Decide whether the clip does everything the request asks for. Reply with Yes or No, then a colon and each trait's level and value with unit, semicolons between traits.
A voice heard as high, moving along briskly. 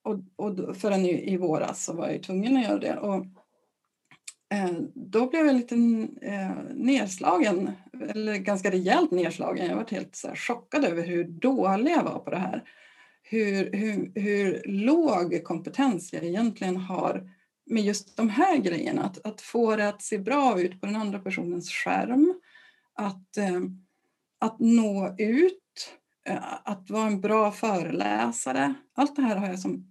No: high, 210 Hz; average, 155 wpm